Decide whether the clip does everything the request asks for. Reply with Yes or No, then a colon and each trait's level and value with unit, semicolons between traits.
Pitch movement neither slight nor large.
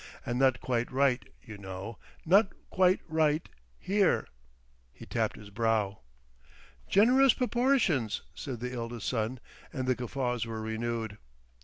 No: wide, 6.1 semitones